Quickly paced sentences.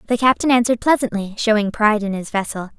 No: average, 195 wpm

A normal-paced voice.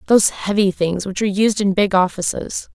Yes: average, 195 wpm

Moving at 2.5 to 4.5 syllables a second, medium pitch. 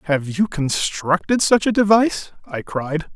Yes: 4.4 syllables/s; medium, 175 Hz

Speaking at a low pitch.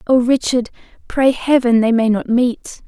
No: high, 245 Hz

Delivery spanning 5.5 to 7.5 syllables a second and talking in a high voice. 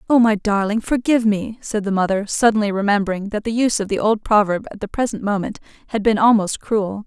Yes: 6.0 syllables/s; high, 210 Hz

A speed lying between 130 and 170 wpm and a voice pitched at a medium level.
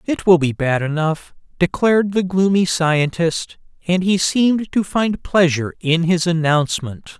Yes: average, 150 wpm; medium, 170 Hz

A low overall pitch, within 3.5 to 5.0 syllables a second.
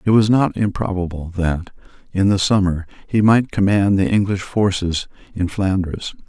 Yes: very low, 95 Hz; 4.6 syllables/s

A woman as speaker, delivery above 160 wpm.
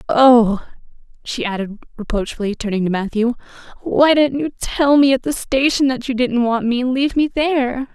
Yes: female; average, 180 wpm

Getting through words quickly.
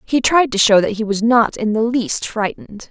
Yes: fast, 250 wpm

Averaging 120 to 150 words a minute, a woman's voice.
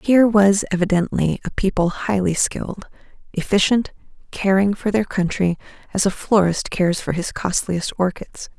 Yes: average, 140 wpm; female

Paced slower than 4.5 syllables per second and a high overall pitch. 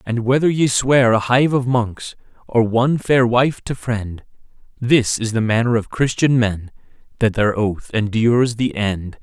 No: 4.2 syllables/s; low, 120 Hz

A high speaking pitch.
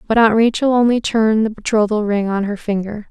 Yes: high, 215 Hz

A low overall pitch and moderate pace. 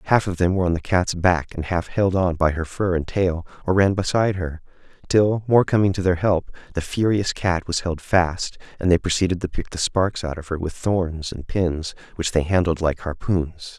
No: very low, 90 Hz; fast, 225 wpm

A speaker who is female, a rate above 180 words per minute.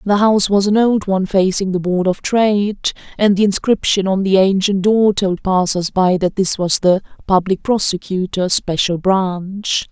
No: female; average, 175 wpm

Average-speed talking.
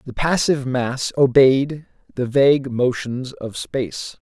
No: slow, 125 wpm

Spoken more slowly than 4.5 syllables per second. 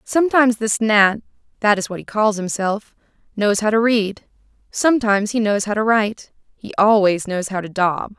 No: 5.1 syllables/s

